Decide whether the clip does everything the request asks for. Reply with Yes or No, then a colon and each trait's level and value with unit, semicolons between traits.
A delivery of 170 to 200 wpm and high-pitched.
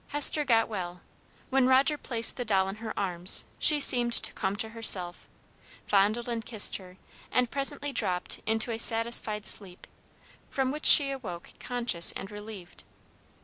No: average, 155 wpm; high, 225 Hz